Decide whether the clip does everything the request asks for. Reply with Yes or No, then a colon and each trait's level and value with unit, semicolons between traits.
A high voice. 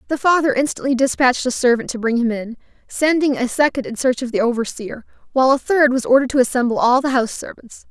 Yes: very high, 255 Hz